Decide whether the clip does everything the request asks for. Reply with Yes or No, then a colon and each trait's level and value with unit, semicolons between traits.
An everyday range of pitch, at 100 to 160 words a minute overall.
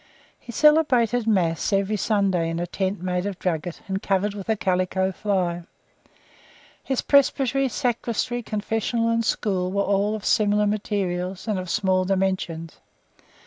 Yes: average, 3.3 semitones; average, 145 wpm